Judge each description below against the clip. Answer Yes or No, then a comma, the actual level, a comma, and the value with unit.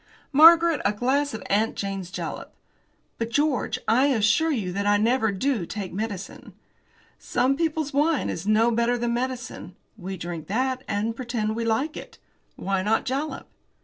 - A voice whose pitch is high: Yes, high, 235 Hz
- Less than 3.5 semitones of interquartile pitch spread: No, average, 4.7 semitones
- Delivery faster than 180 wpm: No, average, 160 wpm